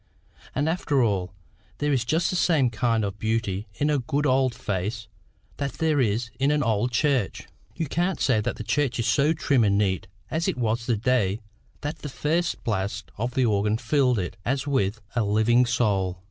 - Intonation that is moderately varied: Yes, average, 5.0 semitones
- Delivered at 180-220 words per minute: Yes, average, 190 wpm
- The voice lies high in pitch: No, low, 120 Hz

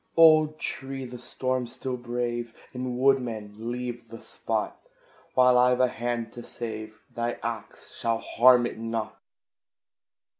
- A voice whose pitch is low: Yes, low, 120 Hz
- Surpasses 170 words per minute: No, slow, 135 wpm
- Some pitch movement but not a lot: No, narrow, 1.7 semitones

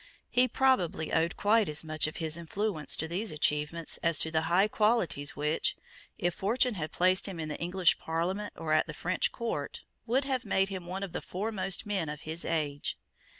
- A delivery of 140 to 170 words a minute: No, average, 195 wpm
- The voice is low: No, medium, 175 Hz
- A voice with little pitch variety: No, average, 4.6 semitones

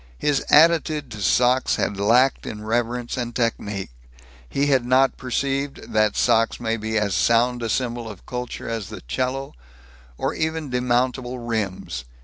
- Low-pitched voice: Yes, low, 120 Hz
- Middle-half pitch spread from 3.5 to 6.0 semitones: No, average, 2.8 semitones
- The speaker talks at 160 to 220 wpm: No, average, 150 wpm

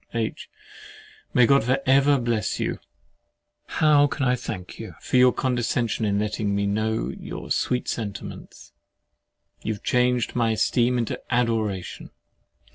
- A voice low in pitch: Yes, low, 120 Hz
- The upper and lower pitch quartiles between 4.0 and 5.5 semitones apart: No, average, 2.7 semitones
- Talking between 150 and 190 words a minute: No, slow, 135 wpm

